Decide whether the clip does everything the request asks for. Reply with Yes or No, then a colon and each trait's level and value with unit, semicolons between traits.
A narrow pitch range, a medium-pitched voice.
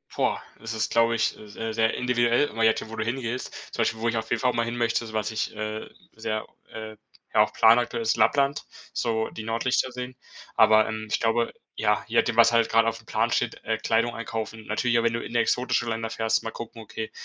No: narrow, 1.1 semitones; low, 115 Hz